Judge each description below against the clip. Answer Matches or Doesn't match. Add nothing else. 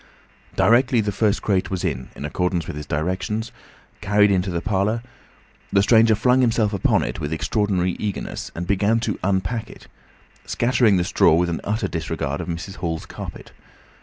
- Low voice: Matches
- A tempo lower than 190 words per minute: Matches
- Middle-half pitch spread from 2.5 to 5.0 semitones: Matches